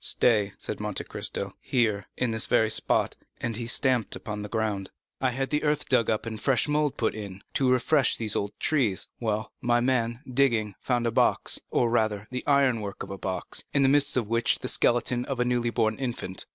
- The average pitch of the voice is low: Yes, low, 115 Hz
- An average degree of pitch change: Yes, average, 3.0 semitones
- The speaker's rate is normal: No, fast, 215 wpm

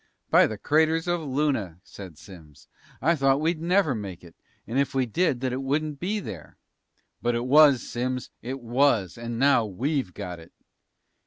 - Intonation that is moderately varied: No, wide, 5.8 semitones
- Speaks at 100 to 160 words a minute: No, average, 175 wpm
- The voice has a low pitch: Yes, low, 130 Hz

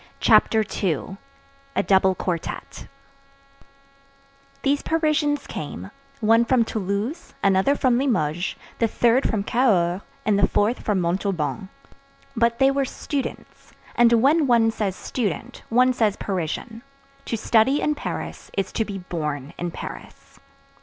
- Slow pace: Yes, slow, 125 wpm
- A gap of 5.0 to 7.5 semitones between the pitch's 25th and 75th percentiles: Yes, average, 5.3 semitones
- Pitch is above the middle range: Yes, high, 225 Hz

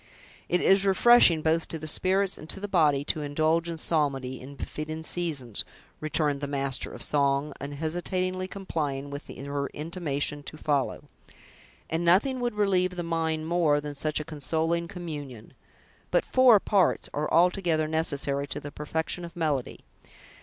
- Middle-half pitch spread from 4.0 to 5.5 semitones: No, average, 3.4 semitones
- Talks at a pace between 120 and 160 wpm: Yes, average, 155 wpm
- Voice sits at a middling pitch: Yes, medium, 155 Hz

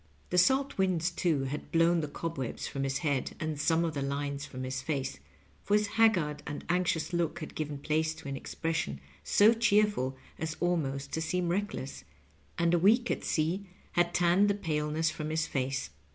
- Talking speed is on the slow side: No, average, 185 wpm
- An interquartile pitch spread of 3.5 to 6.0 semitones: Yes, average, 3.8 semitones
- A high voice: No, medium, 160 Hz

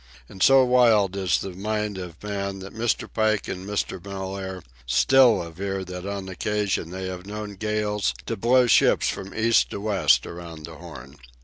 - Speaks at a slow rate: No, average, 175 wpm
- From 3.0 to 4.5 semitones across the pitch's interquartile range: No, narrow, 2.4 semitones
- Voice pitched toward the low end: Yes, low, 100 Hz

